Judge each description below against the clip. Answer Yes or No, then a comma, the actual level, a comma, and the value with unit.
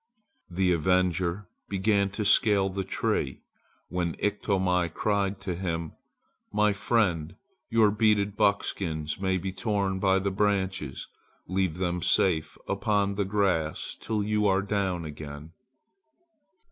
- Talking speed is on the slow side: Yes, slow, 120 wpm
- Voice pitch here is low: Yes, very low, 95 Hz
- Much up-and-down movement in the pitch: No, narrow, 2.5 semitones